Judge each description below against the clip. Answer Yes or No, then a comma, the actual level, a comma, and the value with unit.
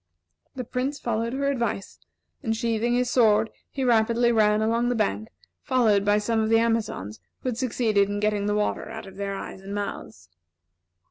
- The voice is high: Yes, high, 220 Hz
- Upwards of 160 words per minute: Yes, average, 185 wpm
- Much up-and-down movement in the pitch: No, narrow, 2.6 semitones